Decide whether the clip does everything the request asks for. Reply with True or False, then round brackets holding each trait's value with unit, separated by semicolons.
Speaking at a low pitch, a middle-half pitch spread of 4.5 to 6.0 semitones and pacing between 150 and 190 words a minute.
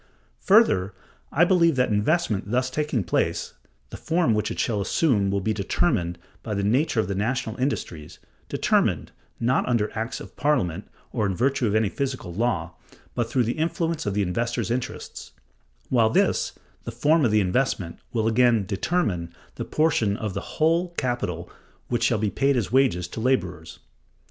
True (115 Hz; 5.0 semitones; 170 wpm)